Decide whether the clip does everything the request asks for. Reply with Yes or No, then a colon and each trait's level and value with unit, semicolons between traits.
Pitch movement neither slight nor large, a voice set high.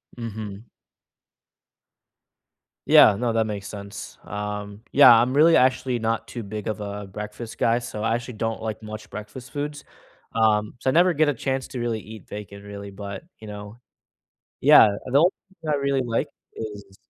No: average, 3.4 semitones; low, 110 Hz